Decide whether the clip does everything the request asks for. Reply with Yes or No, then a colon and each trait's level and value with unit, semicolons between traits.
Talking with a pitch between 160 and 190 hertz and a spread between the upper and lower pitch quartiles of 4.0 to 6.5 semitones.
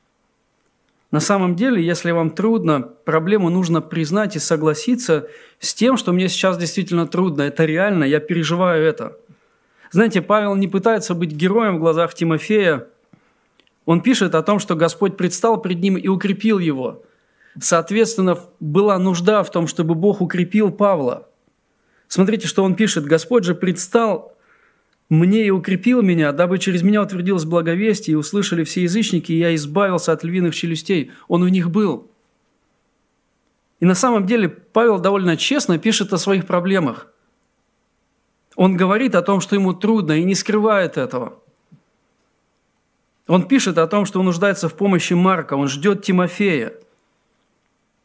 No: medium, 185 Hz; average, 3.4 semitones